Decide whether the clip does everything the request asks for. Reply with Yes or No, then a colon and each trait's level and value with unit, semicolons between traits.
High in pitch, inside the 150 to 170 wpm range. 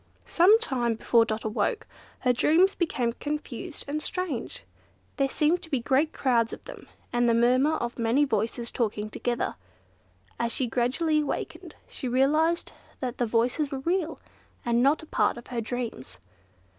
Yes: very high, 255 Hz; average, 160 wpm